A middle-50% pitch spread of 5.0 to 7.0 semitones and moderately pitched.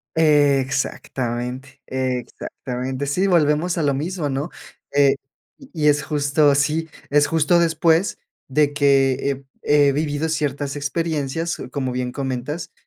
No: average, 2.8 semitones; medium, 145 Hz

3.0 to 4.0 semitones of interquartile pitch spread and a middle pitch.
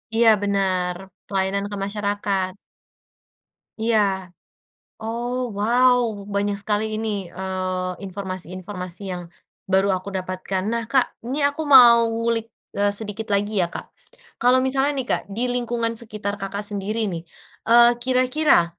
No: average, 3.6 semitones; high, 205 Hz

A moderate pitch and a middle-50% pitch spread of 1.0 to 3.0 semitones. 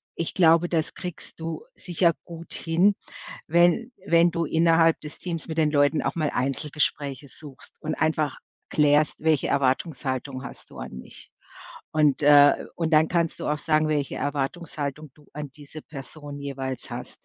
Yes: medium, 155 Hz; narrow, 2.5 semitones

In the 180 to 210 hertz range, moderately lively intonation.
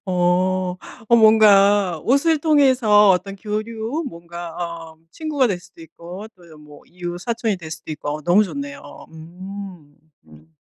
Yes: medium, 185 Hz; average, 4.6 semitones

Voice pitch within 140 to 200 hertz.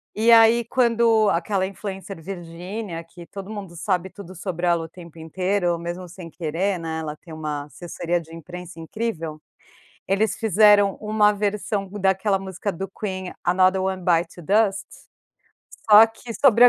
Yes: high, 190 Hz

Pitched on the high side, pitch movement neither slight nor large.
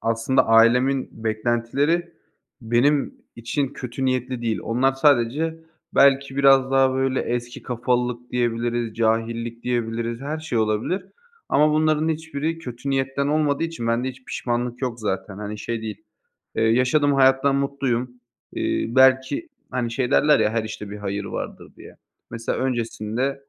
No: low, 125 Hz; average, 3.0 semitones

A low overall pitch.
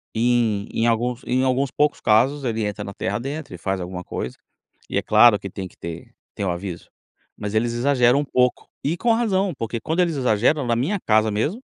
Yes: low, 120 Hz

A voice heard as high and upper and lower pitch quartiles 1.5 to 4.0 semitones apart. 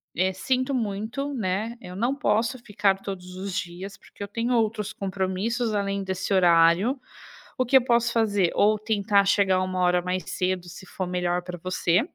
Yes: high, 195 Hz; average, 3.5 semitones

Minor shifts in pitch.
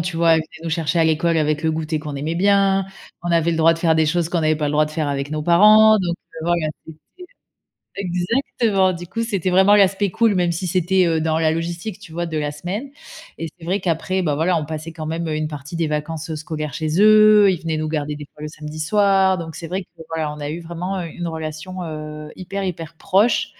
No: average, 3.0 semitones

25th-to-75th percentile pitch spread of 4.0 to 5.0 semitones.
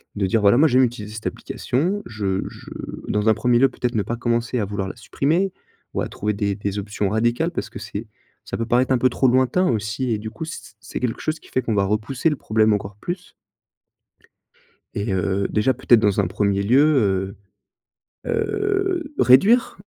Yes: average, 4.5 semitones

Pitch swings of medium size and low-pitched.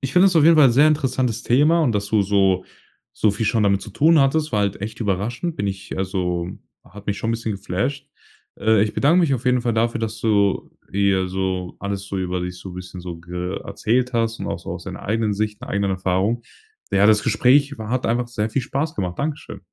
Yes: average, 4.6 semitones; low, 110 Hz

